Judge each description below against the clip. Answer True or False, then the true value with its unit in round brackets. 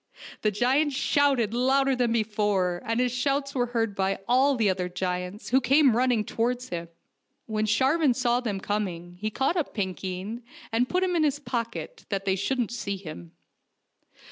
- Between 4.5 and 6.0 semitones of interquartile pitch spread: True (4.9 semitones)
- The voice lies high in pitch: True (230 Hz)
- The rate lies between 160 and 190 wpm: True (170 wpm)